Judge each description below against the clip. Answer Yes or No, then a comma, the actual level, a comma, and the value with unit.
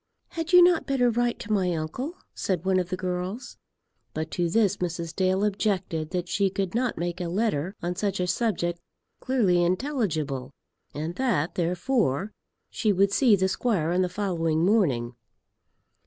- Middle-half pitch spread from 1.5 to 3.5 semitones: No, average, 4.1 semitones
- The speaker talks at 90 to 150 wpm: No, average, 165 wpm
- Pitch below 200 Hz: Yes, medium, 185 Hz